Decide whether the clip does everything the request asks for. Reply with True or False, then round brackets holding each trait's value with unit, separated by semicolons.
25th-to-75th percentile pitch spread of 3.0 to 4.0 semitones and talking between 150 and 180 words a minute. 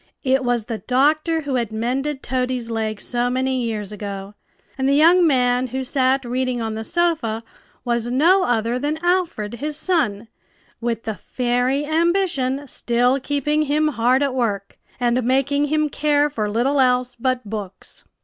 True (3.6 semitones; 160 wpm)